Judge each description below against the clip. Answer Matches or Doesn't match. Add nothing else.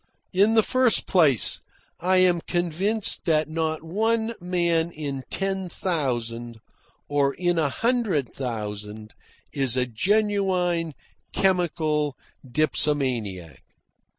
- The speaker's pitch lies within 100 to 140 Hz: Doesn't match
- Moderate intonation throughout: Doesn't match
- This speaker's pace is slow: Matches